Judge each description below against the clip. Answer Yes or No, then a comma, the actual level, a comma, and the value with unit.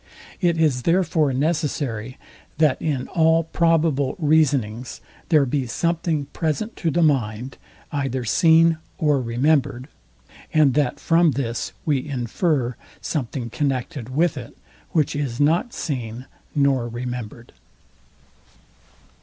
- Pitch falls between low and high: Yes, medium, 145 Hz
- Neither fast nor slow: No, slow, 110 wpm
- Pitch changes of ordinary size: Yes, average, 4.3 semitones